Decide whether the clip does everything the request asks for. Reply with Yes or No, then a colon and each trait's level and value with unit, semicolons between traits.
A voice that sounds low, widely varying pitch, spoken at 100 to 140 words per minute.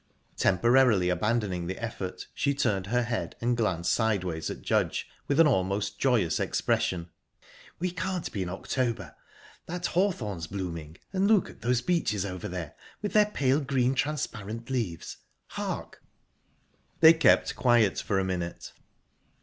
Yes: low, 115 Hz; wide, 6.8 semitones; slow, 135 wpm